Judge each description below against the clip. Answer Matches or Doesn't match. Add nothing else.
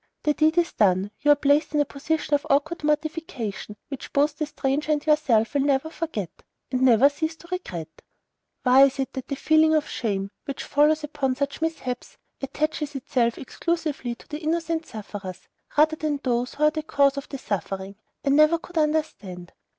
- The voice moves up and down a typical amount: Matches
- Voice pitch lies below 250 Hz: Doesn't match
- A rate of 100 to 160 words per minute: Doesn't match